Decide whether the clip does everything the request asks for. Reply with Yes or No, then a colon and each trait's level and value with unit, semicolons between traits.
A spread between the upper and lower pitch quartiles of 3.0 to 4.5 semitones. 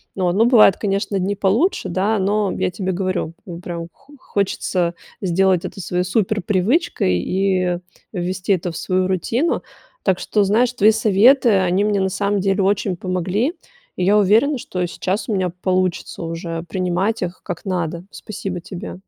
No: narrow, 2.5 semitones